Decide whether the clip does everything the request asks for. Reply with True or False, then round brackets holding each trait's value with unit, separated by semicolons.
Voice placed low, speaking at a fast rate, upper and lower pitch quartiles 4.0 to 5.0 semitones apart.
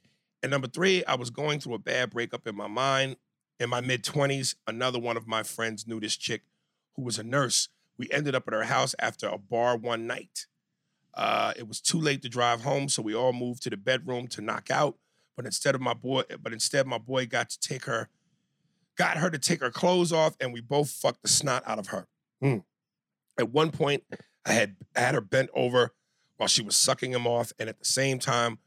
False (125 Hz; 230 wpm; 2.8 semitones)